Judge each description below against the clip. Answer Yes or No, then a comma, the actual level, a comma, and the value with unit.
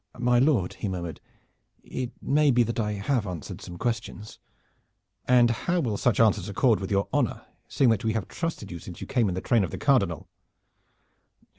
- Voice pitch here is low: Yes, low, 110 Hz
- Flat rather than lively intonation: No, average, 4.0 semitones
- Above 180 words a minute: Yes, average, 190 wpm